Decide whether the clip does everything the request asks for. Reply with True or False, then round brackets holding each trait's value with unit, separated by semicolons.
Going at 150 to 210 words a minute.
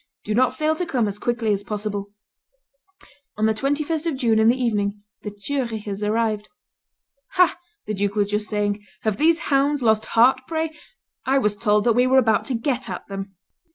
True (190 wpm)